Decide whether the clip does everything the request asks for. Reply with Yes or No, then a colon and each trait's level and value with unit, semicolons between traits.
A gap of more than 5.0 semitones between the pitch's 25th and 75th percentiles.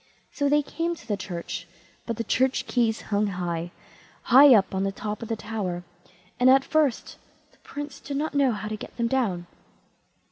Yes: wide, 5.5 semitones